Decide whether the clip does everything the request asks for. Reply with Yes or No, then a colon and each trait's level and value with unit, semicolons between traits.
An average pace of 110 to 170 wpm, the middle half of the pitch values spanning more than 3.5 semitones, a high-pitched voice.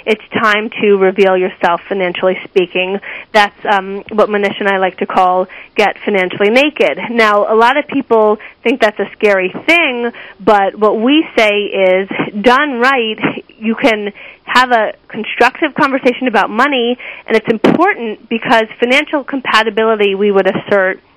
Yes: average, 150 wpm; average, 3.9 semitones; high, 220 Hz